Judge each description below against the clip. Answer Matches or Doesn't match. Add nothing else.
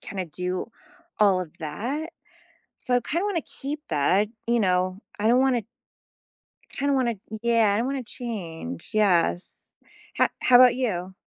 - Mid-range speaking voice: Doesn't match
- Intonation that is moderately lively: Doesn't match